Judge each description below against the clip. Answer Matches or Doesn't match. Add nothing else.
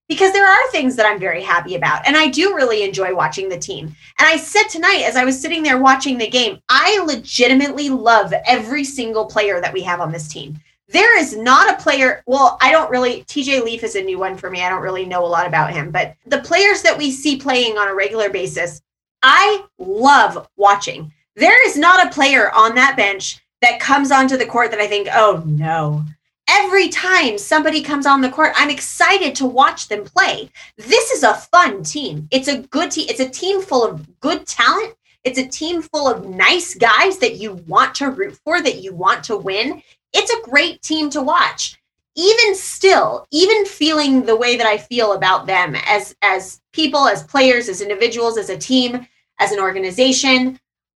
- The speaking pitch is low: Doesn't match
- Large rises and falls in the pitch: Matches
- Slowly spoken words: Doesn't match